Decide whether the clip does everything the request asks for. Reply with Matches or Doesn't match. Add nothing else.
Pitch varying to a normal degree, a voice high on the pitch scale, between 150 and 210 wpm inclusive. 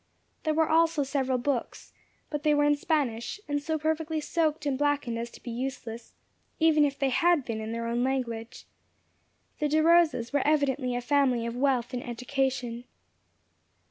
Matches